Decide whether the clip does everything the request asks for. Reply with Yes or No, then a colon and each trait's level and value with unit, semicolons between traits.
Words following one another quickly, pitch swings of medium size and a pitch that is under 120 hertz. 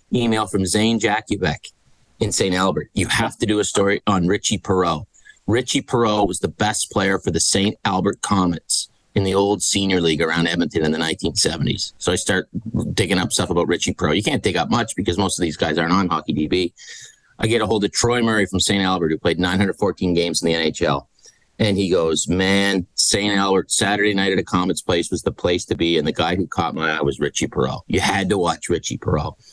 Yes: fast, 220 wpm; average, 3.0 semitones; very low, 95 Hz